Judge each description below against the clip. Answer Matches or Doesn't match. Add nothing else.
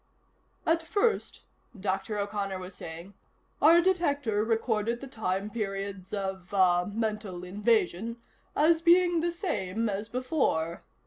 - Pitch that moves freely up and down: Matches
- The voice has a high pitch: Matches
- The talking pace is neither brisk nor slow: Doesn't match